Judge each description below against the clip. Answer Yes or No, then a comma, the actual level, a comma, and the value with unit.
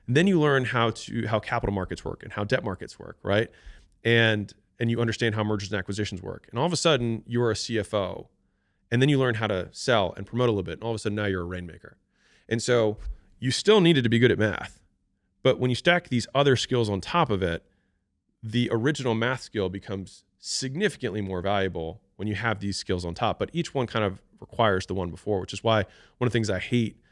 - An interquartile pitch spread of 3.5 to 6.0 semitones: Yes, average, 4.0 semitones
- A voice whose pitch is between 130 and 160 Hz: No, low, 110 Hz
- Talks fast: Yes, fast, 240 wpm